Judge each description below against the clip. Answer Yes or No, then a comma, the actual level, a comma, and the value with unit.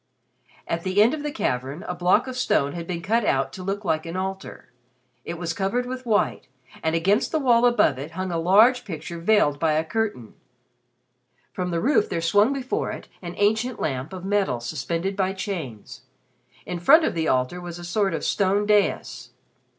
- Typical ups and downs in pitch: Yes, average, 4.3 semitones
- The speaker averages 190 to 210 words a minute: Yes, average, 195 wpm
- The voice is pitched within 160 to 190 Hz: Yes, medium, 185 Hz